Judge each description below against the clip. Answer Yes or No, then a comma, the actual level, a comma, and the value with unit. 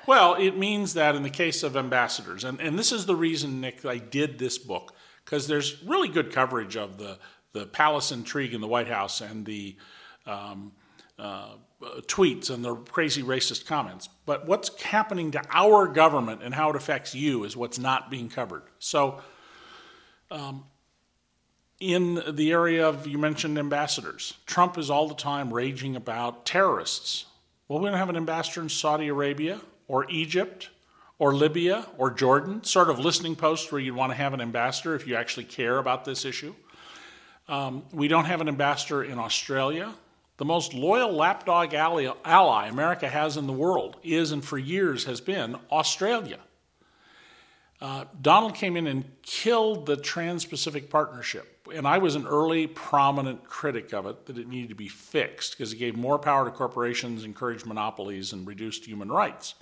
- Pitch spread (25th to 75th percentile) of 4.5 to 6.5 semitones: Yes, average, 4.8 semitones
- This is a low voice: No, medium, 145 Hz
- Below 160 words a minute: No, average, 175 wpm